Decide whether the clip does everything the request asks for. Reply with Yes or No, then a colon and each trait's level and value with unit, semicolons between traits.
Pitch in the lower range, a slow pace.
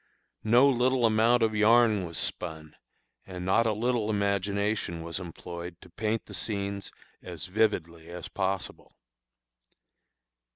Yes: low, 100 Hz; slow, 125 wpm